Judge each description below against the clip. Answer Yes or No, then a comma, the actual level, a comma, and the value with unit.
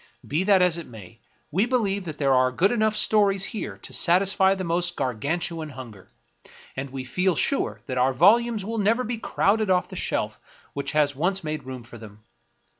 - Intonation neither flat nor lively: No, wide, 7.1 semitones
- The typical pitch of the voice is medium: Yes, medium, 175 Hz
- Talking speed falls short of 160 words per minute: No, average, 190 wpm